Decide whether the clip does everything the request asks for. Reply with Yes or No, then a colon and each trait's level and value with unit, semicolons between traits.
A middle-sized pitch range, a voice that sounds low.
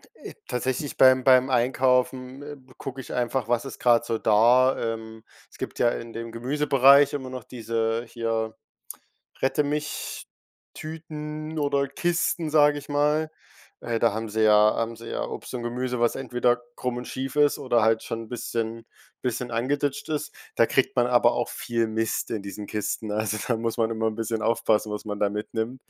Yes: average, 3.0 semitones; low, 120 Hz